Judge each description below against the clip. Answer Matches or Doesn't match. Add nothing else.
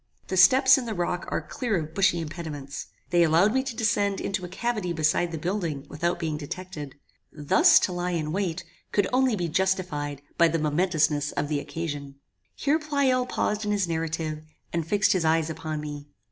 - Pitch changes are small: Doesn't match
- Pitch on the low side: Doesn't match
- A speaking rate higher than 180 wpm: Matches